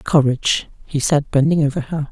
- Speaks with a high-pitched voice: No, medium, 145 Hz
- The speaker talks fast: No, average, 170 wpm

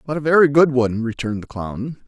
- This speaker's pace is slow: No, fast, 230 wpm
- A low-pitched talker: Yes, low, 130 Hz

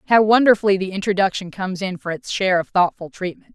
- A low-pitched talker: No, high, 190 Hz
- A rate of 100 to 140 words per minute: No, fast, 205 wpm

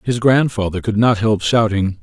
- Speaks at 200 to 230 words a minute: No, average, 180 wpm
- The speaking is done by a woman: No, male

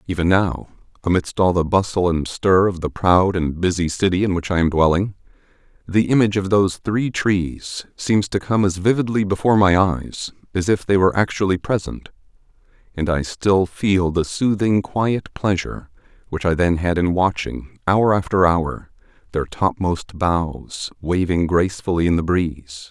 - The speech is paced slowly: No, average, 170 wpm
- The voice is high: No, very low, 90 Hz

